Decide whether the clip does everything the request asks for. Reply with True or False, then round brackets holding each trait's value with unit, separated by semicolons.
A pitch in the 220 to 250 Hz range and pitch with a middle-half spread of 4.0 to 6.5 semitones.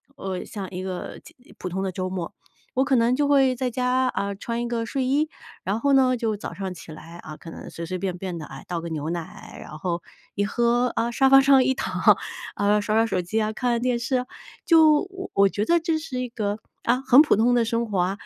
True (225 Hz; 5.4 semitones)